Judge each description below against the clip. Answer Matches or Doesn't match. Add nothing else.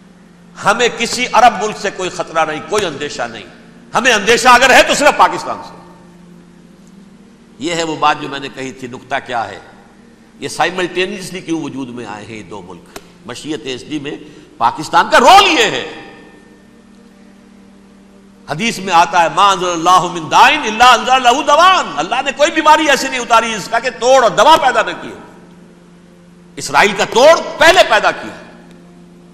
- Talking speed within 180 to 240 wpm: Doesn't match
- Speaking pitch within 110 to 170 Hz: Doesn't match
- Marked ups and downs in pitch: Matches